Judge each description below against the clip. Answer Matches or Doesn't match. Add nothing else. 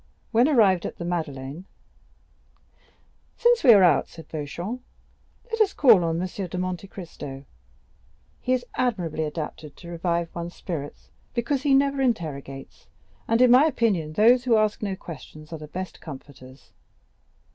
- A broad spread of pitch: Matches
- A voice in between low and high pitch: Matches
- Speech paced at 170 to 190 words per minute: Doesn't match